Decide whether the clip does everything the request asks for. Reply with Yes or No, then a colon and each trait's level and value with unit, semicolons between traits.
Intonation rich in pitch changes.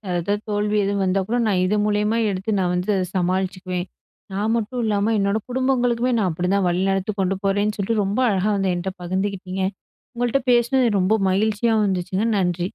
No: average, 2.7 semitones